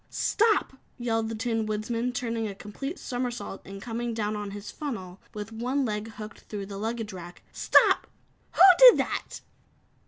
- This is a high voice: Yes, high, 225 Hz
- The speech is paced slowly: No, average, 160 wpm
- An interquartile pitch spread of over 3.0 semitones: No, average, 2.7 semitones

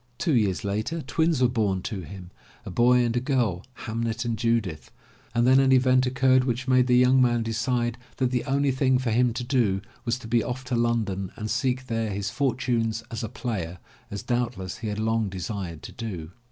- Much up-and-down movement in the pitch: No, average, 2.9 semitones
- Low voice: Yes, low, 120 Hz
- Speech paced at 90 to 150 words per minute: No, fast, 205 wpm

